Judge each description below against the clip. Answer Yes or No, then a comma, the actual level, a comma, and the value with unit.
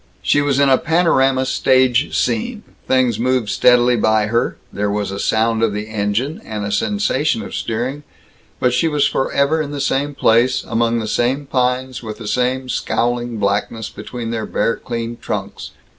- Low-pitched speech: Yes, low, 125 Hz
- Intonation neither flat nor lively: Yes, average, 3.2 semitones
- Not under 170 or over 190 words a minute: Yes, average, 175 wpm